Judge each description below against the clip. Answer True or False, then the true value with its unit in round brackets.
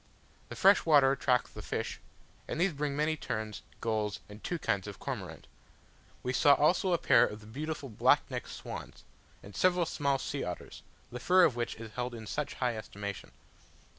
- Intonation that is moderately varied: False (6.0 semitones)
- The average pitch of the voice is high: False (130 Hz)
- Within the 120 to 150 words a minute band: False (185 wpm)